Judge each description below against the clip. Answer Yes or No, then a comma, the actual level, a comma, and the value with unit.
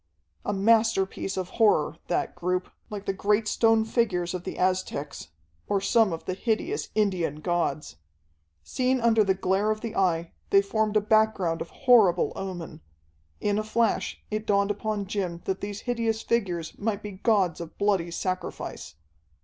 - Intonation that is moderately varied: Yes, average, 3.1 semitones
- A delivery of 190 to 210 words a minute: No, average, 160 wpm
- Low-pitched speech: No, high, 200 Hz